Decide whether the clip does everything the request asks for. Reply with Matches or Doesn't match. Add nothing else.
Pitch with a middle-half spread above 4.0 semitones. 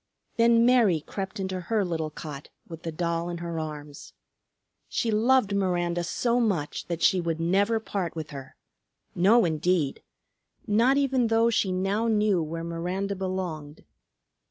Matches